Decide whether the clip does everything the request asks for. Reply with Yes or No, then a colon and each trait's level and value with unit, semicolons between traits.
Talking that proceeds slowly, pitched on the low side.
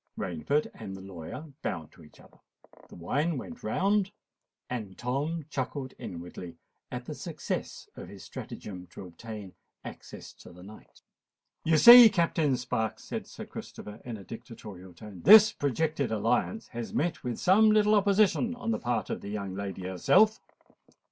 No: average, 160 wpm; low, 125 Hz